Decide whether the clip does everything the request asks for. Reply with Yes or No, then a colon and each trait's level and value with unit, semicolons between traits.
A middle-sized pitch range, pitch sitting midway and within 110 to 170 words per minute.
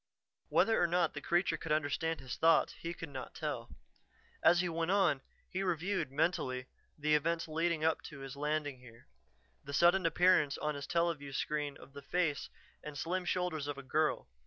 No: average, 3.4 semitones; medium, 155 Hz; average, 180 wpm